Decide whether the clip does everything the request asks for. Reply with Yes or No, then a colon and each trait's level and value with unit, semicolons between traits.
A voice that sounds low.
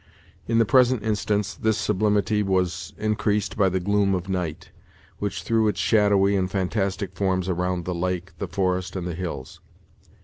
Yes: very low, 95 Hz